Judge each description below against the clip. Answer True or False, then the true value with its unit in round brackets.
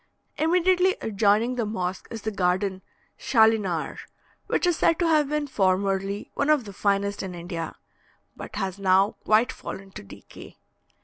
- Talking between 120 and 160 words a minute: True (150 wpm)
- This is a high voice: True (205 Hz)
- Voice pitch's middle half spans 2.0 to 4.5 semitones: False (5.1 semitones)